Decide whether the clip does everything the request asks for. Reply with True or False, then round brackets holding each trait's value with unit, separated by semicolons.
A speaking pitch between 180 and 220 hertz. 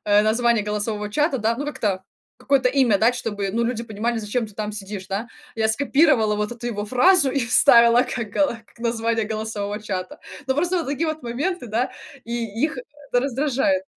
False (235 Hz)